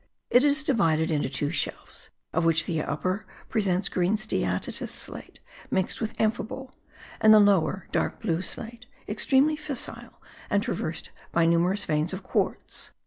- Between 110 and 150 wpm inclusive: Yes, average, 145 wpm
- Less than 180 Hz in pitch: No, high, 195 Hz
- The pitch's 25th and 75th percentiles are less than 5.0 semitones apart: No, wide, 5.4 semitones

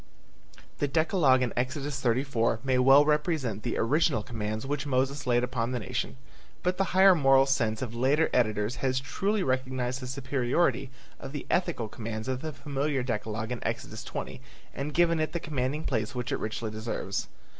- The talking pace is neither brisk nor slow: Yes, average, 175 wpm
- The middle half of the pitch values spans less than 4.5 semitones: Yes, average, 3.6 semitones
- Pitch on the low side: Yes, low, 130 Hz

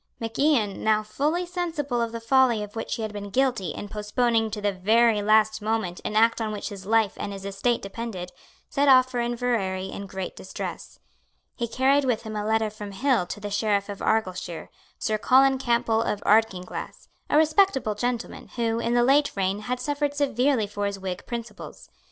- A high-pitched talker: Yes, high, 225 Hz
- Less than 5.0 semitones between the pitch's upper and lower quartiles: Yes, average, 3.3 semitones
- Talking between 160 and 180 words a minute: No, average, 195 wpm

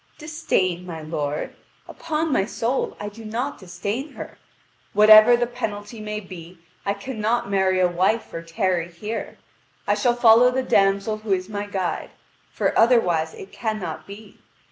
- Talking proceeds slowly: No, average, 155 wpm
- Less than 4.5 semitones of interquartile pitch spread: Yes, average, 4.1 semitones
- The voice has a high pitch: Yes, high, 205 Hz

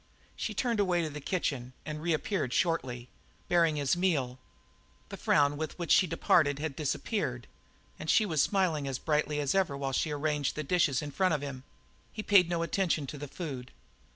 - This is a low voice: No, medium, 155 Hz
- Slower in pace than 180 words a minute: No, average, 185 wpm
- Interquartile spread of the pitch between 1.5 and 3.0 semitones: No, average, 3.9 semitones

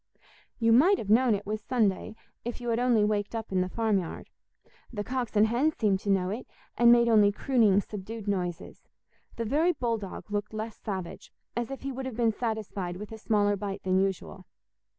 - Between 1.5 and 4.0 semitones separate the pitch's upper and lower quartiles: Yes, average, 2.9 semitones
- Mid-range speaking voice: No, high, 215 Hz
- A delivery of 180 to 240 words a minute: Yes, average, 200 wpm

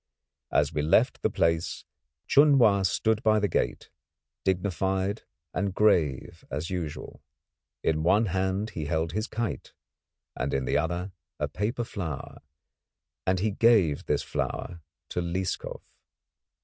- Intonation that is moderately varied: Yes, average, 4.5 semitones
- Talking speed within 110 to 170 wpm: Yes, slow, 135 wpm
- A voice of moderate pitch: No, very low, 95 Hz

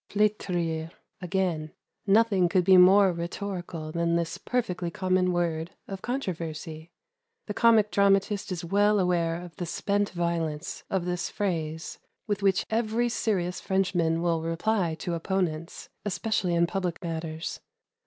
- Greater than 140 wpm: No, slow, 135 wpm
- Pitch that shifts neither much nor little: Yes, average, 3.0 semitones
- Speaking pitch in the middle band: Yes, medium, 180 Hz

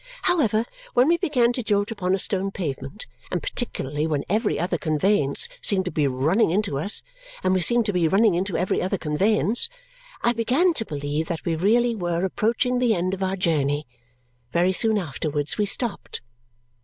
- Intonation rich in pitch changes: Yes, wide, 5.7 semitones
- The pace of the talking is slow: No, average, 180 wpm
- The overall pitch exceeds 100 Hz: Yes, high, 190 Hz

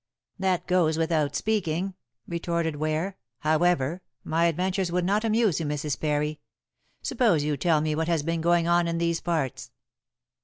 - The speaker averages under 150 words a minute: No, average, 160 wpm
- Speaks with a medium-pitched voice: Yes, medium, 170 Hz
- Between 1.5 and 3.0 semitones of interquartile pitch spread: Yes, narrow, 2.6 semitones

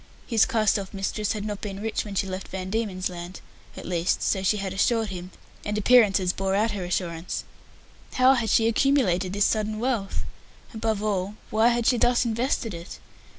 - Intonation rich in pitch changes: No, average, 3.0 semitones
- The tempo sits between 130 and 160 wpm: No, average, 190 wpm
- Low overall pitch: No, high, 205 Hz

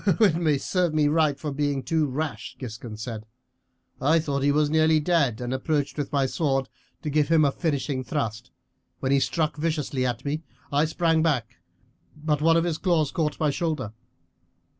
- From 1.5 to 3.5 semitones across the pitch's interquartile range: Yes, average, 2.9 semitones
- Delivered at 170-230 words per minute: Yes, average, 180 wpm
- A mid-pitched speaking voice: Yes, medium, 150 Hz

